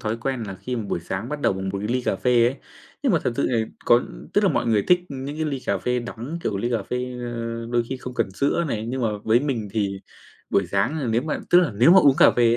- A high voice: No, low, 120 Hz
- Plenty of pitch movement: No, average, 3.4 semitones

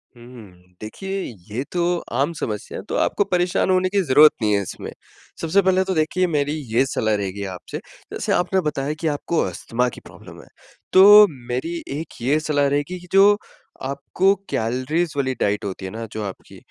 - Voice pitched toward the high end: No, medium, 145 Hz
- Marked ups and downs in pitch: Yes, wide, 7.7 semitones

